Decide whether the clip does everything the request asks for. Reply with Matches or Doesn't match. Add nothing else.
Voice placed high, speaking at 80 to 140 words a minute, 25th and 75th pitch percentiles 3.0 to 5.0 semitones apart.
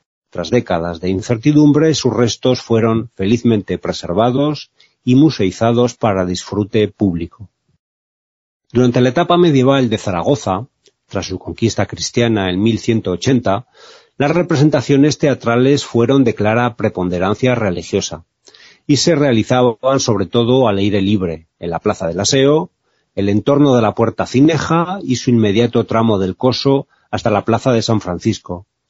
Doesn't match